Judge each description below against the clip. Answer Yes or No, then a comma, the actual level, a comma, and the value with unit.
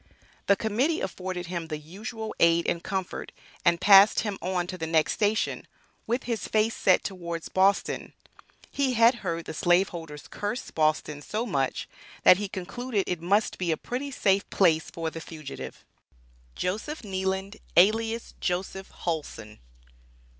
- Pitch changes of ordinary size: Yes, average, 4.2 semitones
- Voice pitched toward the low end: No, high, 190 Hz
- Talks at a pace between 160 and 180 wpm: No, average, 145 wpm